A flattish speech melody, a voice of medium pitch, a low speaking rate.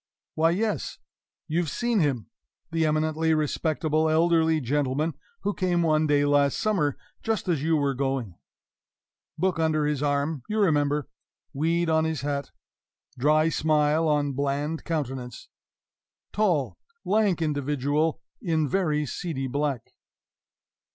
Yes: narrow, 2.3 semitones; medium, 155 Hz; slow, 125 wpm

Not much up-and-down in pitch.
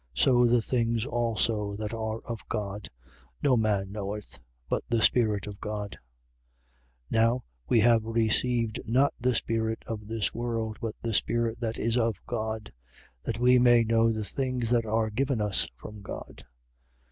Yes: narrow, 1.7 semitones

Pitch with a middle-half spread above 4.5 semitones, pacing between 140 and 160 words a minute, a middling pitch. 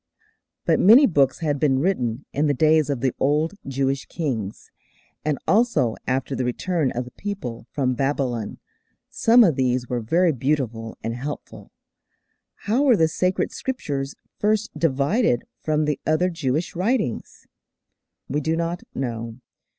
Yes: average, 5.0 semitones; average, 145 wpm; medium, 145 Hz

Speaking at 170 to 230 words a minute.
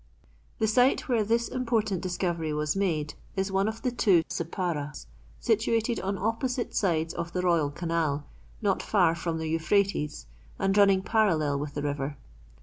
No: average, 155 wpm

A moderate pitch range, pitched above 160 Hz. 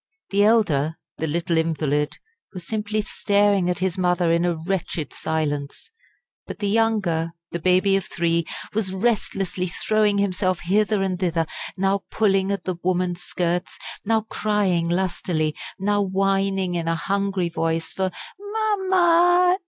Yes: average, 3.3 semitones; high, 190 Hz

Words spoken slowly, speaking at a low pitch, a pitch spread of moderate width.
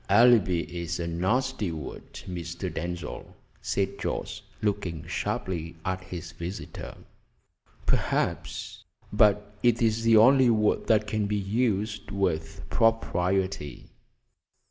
Yes: slow, 110 wpm; very low, 95 Hz; average, 4.0 semitones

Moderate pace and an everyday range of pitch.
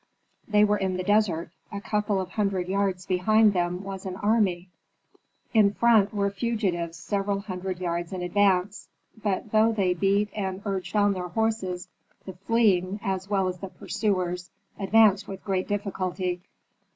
No: average, 155 wpm; narrow, 2.1 semitones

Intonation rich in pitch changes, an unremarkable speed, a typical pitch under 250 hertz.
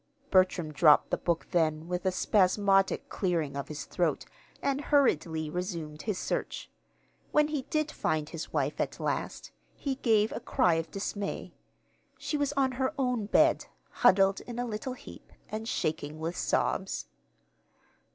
Yes: wide, 7.4 semitones; average, 150 wpm; high, 190 Hz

